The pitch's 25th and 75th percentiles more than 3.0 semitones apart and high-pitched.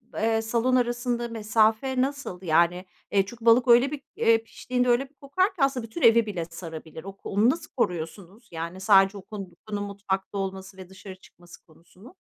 Yes: average, 4.3 semitones; high, 215 Hz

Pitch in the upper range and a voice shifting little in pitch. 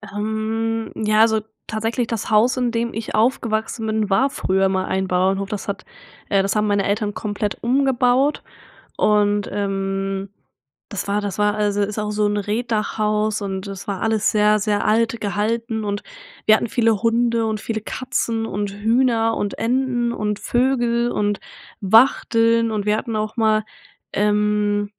Yes: high, 215 Hz; narrow, 1.9 semitones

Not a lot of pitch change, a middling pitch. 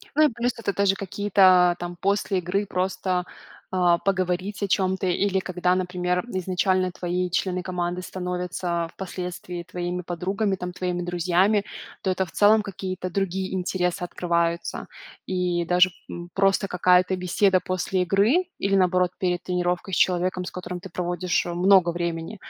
Yes: narrow, 1.4 semitones; medium, 180 Hz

